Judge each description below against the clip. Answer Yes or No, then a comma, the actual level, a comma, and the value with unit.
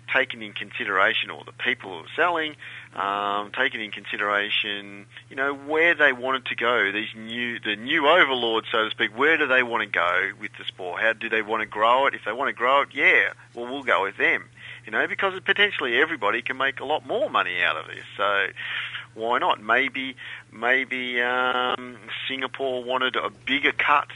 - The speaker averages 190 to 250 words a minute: Yes, average, 200 wpm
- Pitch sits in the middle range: No, low, 125 Hz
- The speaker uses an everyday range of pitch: Yes, average, 3.2 semitones